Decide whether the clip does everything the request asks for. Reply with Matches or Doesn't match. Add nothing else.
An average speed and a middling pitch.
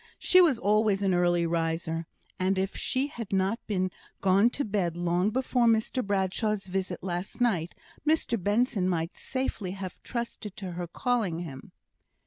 Doesn't match